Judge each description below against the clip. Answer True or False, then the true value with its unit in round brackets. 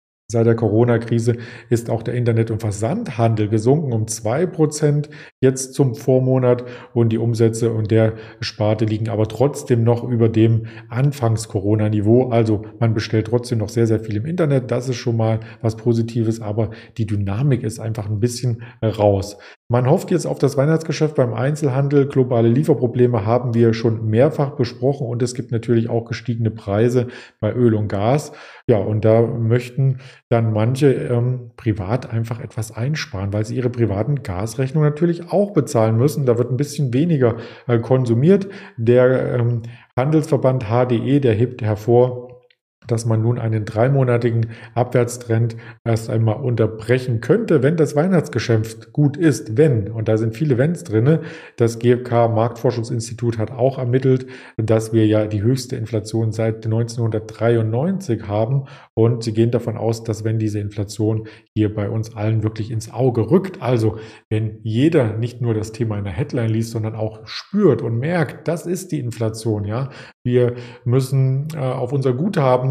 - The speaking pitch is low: True (120 Hz)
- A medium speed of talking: True (160 wpm)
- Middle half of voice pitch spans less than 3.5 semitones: True (2.8 semitones)